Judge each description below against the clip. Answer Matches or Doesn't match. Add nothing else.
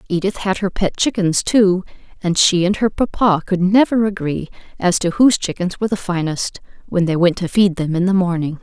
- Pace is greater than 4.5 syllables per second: Matches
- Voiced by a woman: Matches